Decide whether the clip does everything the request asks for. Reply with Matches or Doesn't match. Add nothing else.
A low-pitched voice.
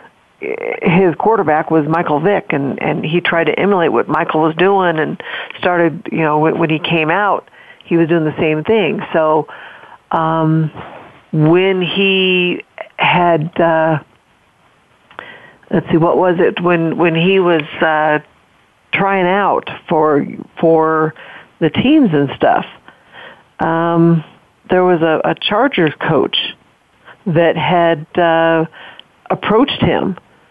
Doesn't match